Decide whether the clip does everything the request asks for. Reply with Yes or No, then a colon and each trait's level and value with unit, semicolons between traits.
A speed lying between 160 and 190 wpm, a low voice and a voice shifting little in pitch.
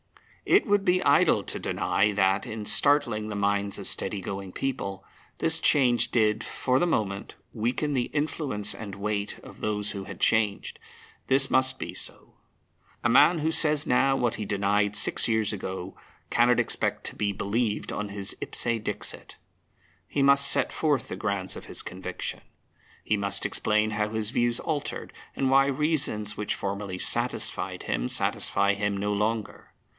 No: average, 165 wpm; low, 105 Hz; average, 4.8 semitones